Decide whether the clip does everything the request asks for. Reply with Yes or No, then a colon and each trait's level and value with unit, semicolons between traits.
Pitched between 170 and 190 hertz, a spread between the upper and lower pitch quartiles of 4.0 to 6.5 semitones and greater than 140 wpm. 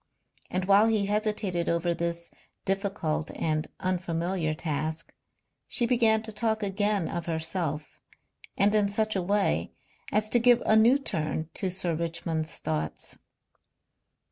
No: medium, 185 Hz; average, 4.3 semitones; slow, 135 wpm